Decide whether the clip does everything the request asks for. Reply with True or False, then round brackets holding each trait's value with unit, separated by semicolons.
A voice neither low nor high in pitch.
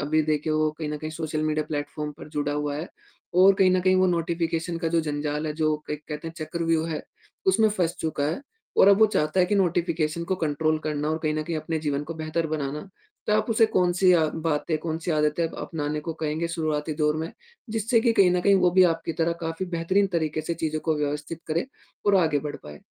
True (160 Hz)